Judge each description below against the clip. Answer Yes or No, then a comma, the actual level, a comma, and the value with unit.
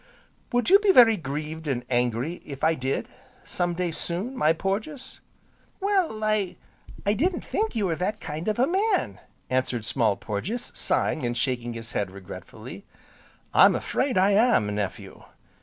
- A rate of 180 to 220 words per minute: No, average, 155 wpm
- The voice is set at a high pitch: No, medium, 170 Hz